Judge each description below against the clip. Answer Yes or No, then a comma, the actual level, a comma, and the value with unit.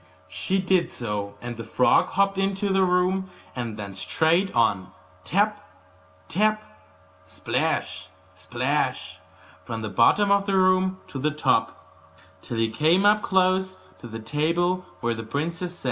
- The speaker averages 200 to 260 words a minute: No, average, 145 wpm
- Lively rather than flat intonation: Yes, wide, 8.3 semitones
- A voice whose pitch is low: No, medium, 180 Hz